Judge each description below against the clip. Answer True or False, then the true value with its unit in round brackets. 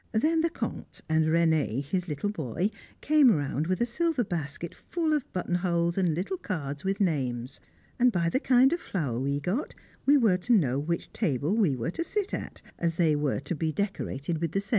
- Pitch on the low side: False (175 Hz)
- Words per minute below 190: False (205 wpm)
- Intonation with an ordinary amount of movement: False (7.2 semitones)